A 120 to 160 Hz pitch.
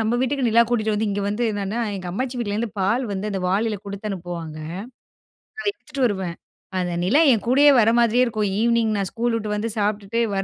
No: high, 215 Hz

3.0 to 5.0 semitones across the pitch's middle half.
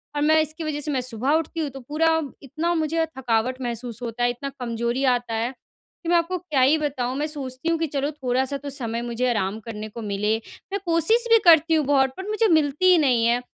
Yes: average, 4.7 semitones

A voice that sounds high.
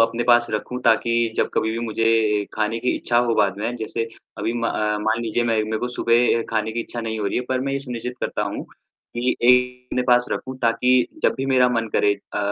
No: low, 115 Hz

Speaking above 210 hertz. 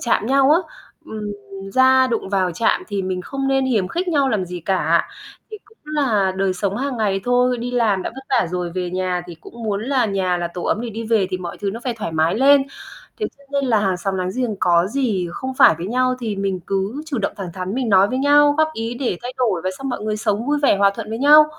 Yes: high, 220 Hz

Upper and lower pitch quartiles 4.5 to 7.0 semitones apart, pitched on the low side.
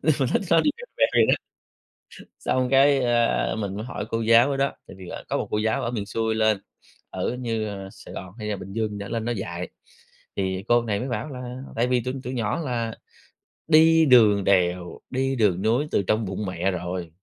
No: average, 4.1 semitones; low, 115 Hz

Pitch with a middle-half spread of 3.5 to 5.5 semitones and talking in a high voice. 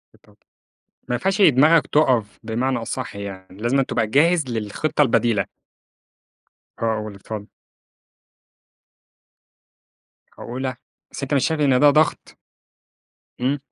No: average, 4.8 semitones; low, 130 Hz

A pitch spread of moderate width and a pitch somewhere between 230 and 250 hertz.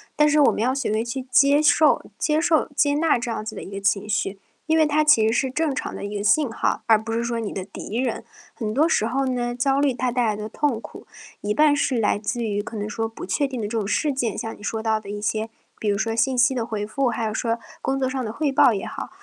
Yes: average, 4.0 semitones; high, 235 Hz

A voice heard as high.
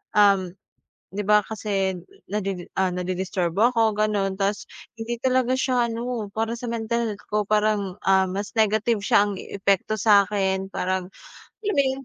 Yes: high, 210 Hz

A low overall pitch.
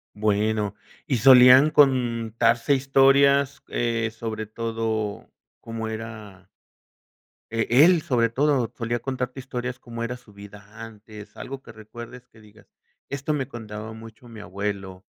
Yes: low, 115 Hz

